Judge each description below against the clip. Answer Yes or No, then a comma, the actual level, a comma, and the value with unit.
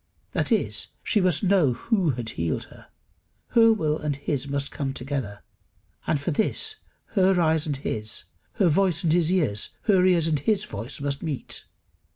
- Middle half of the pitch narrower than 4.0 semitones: No, average, 5.2 semitones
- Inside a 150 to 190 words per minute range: Yes, average, 175 wpm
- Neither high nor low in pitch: Yes, medium, 155 Hz